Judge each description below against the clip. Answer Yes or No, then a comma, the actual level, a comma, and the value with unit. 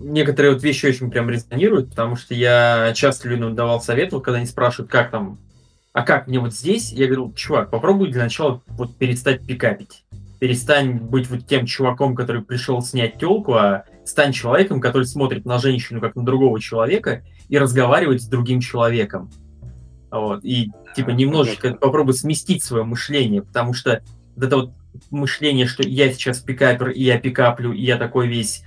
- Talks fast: Yes, fast, 175 wpm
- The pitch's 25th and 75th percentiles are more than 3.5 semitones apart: No, narrow, 2.4 semitones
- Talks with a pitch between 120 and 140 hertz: Yes, low, 125 Hz